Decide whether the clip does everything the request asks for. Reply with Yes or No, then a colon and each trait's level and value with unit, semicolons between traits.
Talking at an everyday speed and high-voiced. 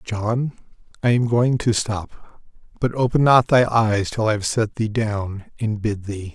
No: average, 190 wpm; low, 110 Hz